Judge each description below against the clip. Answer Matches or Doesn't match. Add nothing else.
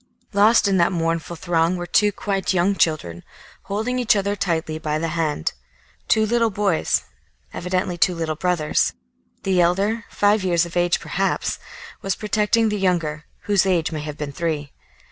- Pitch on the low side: Doesn't match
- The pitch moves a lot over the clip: Doesn't match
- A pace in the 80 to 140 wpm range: Doesn't match